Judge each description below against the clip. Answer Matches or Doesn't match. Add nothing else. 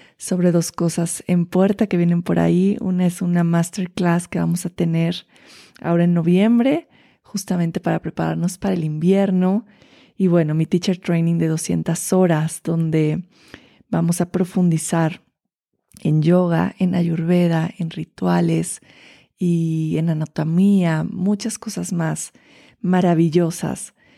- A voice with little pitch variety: Matches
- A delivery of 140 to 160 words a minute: Doesn't match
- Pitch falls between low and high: Matches